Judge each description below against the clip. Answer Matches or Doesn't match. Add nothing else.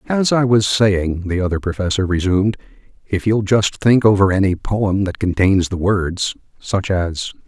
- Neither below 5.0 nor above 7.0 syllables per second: Doesn't match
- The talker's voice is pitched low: Matches